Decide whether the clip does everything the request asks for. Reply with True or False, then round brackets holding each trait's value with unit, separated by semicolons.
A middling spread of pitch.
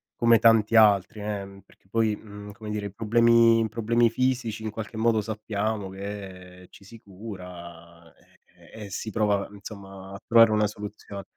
False (2.2 semitones)